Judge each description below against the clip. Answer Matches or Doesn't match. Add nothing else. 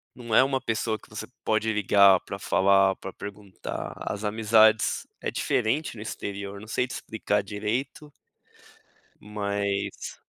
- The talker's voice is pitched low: Matches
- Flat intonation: Matches